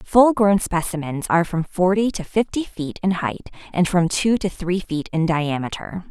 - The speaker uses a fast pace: No, average, 185 wpm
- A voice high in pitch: No, medium, 180 Hz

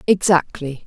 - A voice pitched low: No, medium, 165 Hz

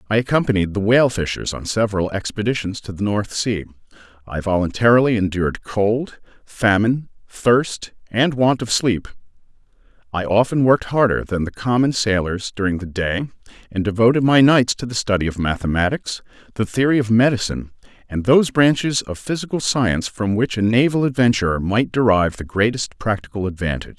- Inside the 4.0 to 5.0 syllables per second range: No, 5.6 syllables/s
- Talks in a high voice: No, low, 110 Hz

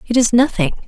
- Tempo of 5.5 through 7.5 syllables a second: Yes, 6.4 syllables/s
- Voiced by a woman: Yes, female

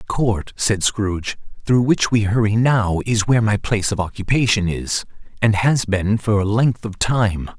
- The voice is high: No, low, 105 Hz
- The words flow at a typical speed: Yes, average, 190 wpm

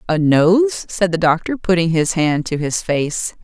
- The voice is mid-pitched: Yes, medium, 160 Hz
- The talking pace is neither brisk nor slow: Yes, average, 190 wpm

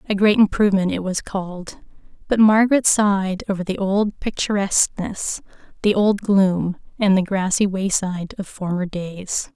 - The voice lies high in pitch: Yes, high, 195 Hz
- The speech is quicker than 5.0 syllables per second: No, 4.7 syllables/s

